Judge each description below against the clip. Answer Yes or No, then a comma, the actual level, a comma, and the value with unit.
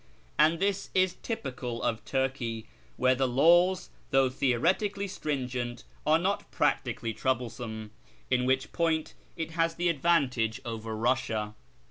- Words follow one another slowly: Yes, slow, 130 wpm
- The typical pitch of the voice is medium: No, low, 130 Hz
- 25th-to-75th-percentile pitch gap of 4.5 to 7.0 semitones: Yes, wide, 5.6 semitones